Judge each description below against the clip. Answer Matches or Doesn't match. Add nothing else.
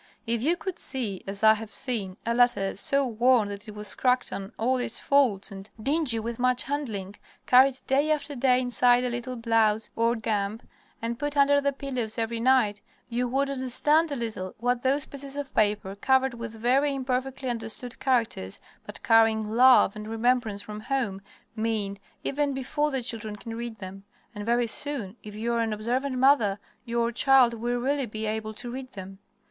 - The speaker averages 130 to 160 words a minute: Doesn't match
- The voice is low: Doesn't match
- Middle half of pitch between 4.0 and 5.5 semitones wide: Doesn't match